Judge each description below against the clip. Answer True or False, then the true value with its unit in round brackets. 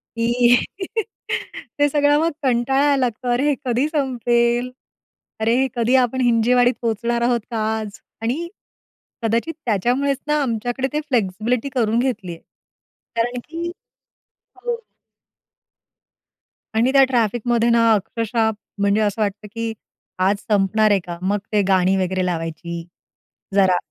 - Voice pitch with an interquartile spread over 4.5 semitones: False (3.3 semitones)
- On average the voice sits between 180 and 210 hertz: False (235 Hz)